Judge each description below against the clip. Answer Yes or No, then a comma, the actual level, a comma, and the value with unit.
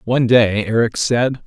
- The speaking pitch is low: Yes, low, 115 Hz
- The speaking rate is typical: Yes, average, 165 wpm